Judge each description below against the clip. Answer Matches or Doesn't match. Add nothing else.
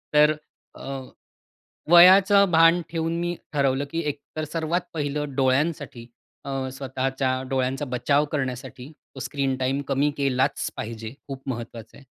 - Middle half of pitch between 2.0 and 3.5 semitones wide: Matches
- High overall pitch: Doesn't match